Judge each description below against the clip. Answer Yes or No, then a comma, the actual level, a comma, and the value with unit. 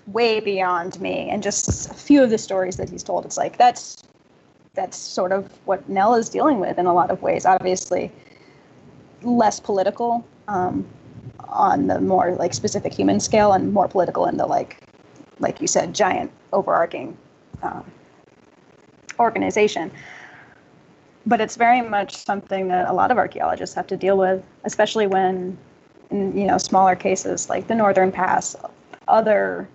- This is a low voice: No, high, 195 Hz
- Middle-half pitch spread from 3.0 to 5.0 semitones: No, narrow, 2.6 semitones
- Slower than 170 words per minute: Yes, average, 160 wpm